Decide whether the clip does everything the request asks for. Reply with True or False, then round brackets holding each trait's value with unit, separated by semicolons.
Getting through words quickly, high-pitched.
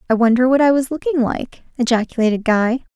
False (185 wpm; 245 Hz)